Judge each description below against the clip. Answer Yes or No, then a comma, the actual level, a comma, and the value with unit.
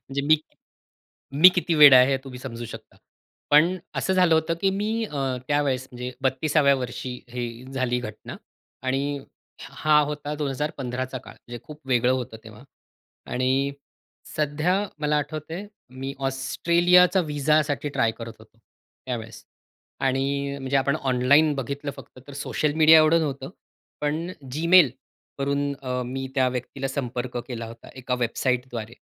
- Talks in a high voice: No, medium, 140 Hz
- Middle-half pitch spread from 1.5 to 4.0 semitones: Yes, average, 3.0 semitones